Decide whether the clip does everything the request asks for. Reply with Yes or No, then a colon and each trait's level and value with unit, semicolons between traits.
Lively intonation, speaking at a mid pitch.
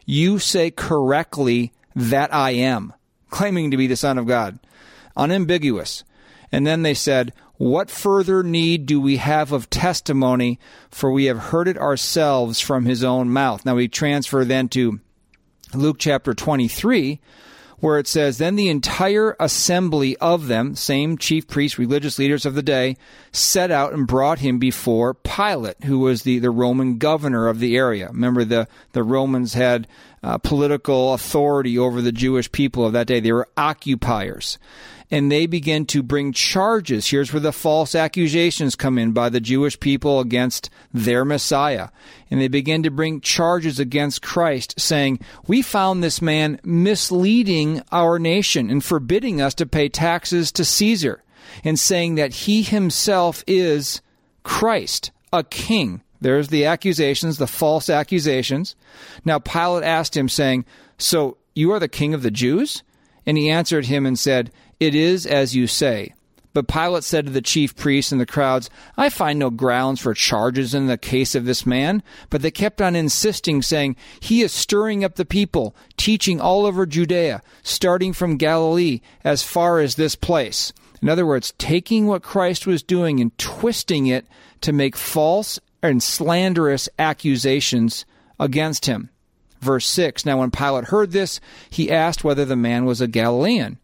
No: average, 4.6 semitones; medium, 145 Hz